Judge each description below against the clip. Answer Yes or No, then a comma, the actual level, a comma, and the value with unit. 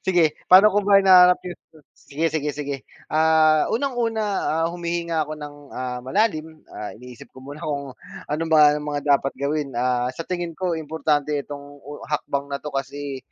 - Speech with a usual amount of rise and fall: Yes, average, 3.2 semitones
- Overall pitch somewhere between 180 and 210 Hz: No, medium, 150 Hz